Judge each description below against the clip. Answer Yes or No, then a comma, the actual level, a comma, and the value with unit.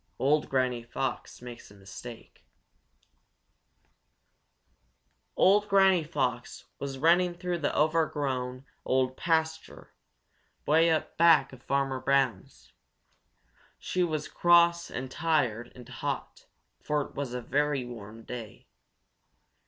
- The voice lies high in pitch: No, medium, 140 Hz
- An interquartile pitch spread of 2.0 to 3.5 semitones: No, average, 4.6 semitones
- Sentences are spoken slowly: Yes, slow, 110 wpm